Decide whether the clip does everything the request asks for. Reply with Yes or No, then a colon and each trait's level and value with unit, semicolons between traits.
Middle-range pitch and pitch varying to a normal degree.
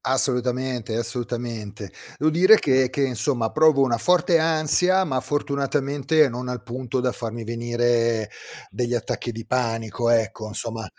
No: low, 125 Hz; average, 3.2 semitones